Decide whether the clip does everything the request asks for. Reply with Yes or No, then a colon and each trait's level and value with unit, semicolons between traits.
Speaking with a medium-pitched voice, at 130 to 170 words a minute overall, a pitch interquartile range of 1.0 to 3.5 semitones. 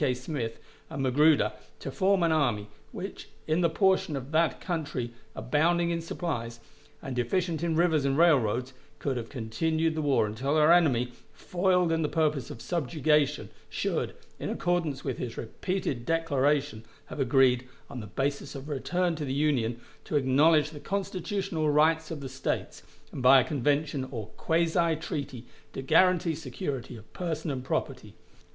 No: medium, 150 Hz; average, 165 wpm; average, 4.1 semitones